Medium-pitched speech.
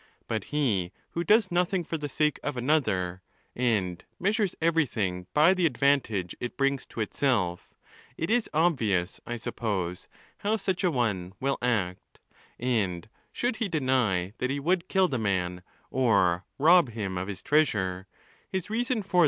No: low, 125 Hz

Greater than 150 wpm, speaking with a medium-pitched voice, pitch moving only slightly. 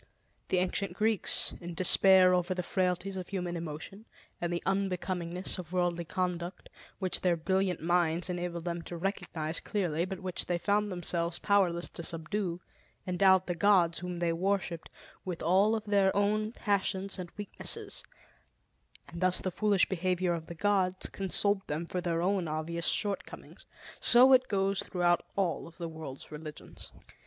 Yes: average, 160 wpm; medium, 180 Hz; narrow, 2.2 semitones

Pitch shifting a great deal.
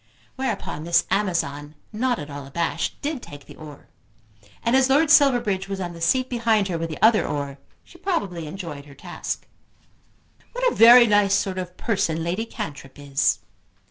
Yes: wide, 7.1 semitones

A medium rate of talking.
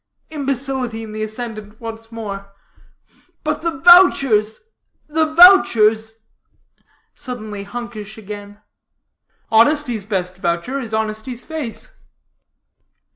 No: slow, 90 wpm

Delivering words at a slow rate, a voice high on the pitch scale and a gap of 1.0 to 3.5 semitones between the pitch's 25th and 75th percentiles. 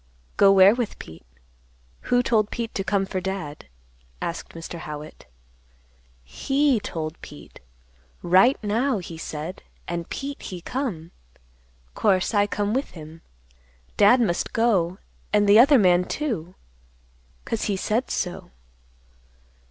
No: slow, 130 wpm; high, 195 Hz; average, 5.1 semitones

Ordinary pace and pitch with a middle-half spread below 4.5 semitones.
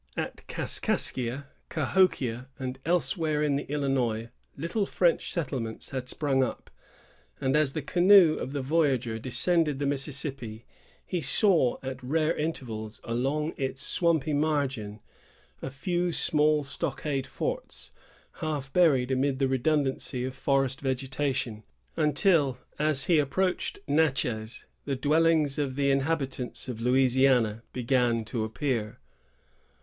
No: slow, 125 wpm; average, 3.2 semitones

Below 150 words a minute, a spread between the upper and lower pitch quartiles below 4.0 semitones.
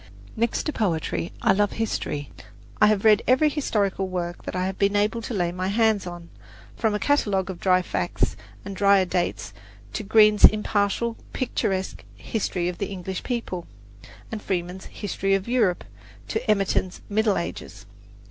No: average, 160 wpm; average, 2.9 semitones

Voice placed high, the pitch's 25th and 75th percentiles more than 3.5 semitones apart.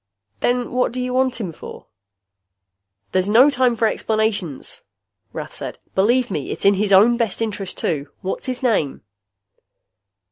Yes: high, 220 Hz; average, 4.5 semitones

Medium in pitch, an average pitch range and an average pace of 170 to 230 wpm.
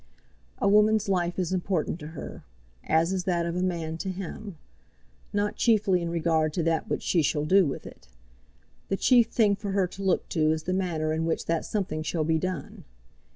Yes: medium, 175 Hz; average, 3.3 semitones; average, 200 wpm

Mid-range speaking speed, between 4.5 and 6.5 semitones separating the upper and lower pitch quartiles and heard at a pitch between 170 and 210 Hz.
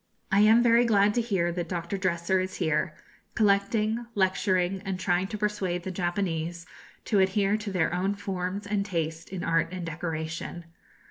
No: average, 165 wpm; average, 2.8 semitones; medium, 185 Hz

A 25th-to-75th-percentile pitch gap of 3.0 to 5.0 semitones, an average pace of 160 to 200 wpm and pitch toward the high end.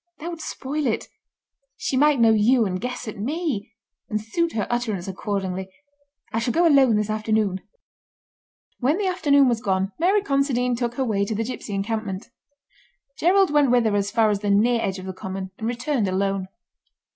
No: wide, 5.5 semitones; average, 185 wpm; high, 230 Hz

